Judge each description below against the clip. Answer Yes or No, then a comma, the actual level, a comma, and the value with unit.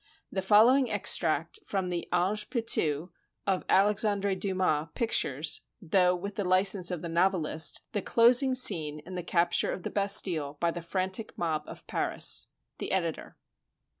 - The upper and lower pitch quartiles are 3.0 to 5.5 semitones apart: Yes, average, 3.3 semitones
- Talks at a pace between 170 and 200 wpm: No, average, 155 wpm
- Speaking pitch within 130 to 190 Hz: Yes, medium, 185 Hz